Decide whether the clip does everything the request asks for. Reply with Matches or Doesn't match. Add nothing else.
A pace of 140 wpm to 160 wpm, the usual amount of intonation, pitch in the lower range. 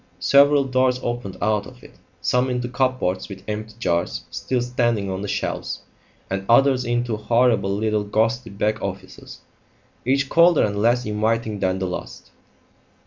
Matches